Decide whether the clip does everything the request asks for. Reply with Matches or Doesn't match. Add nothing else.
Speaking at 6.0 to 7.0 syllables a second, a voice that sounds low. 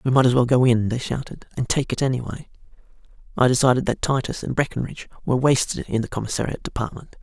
Matches